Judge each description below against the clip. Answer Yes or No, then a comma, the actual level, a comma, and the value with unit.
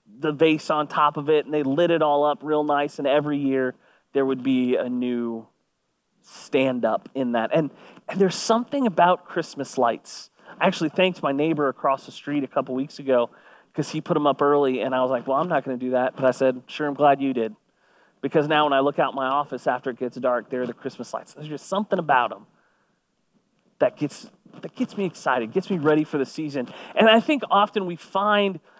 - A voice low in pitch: No, medium, 145 Hz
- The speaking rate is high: Yes, fast, 230 wpm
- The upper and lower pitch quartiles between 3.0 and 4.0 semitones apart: No, average, 4.6 semitones